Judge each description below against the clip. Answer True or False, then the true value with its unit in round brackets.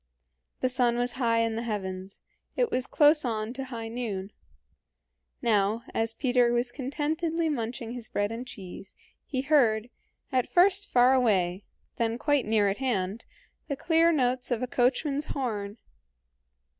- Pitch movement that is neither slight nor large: True (3.4 semitones)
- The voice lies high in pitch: True (245 Hz)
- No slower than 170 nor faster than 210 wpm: False (150 wpm)